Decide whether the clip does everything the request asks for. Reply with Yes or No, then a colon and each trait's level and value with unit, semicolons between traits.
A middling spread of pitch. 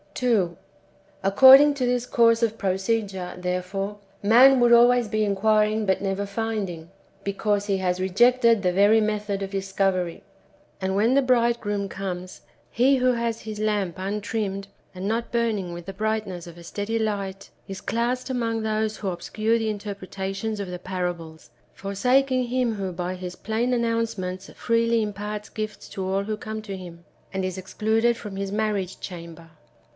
Yes: average, 3.1 semitones